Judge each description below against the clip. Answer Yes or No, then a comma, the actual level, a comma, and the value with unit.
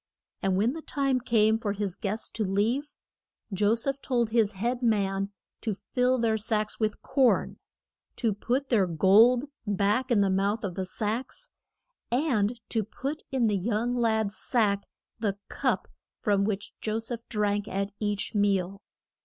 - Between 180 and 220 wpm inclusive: No, average, 160 wpm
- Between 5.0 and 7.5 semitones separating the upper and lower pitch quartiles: No, average, 3.1 semitones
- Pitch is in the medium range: No, high, 215 Hz